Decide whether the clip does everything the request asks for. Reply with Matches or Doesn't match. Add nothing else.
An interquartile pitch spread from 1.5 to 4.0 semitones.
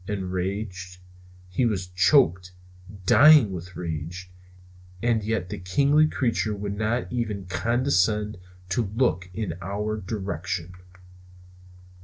Matches